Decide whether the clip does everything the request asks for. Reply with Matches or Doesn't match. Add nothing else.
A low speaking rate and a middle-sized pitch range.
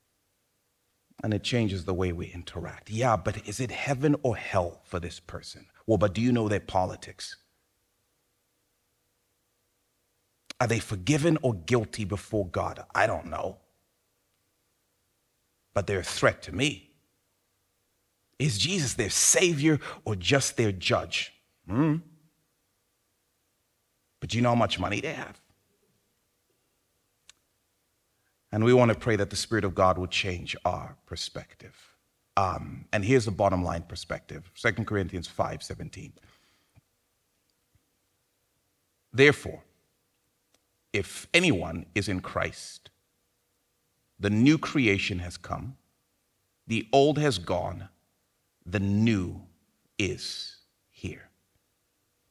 Matches